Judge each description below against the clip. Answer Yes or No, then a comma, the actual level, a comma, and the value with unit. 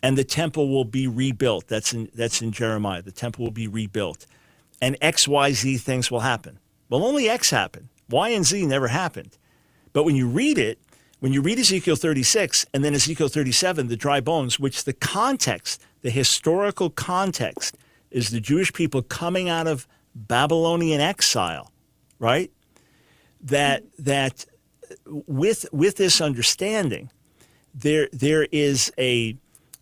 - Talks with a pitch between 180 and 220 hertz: No, medium, 140 Hz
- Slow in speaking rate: No, average, 150 wpm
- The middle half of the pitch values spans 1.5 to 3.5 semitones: No, average, 4.2 semitones